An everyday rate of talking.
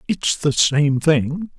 Yes: average, 150 wpm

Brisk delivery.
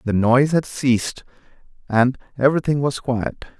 No: slow, 135 wpm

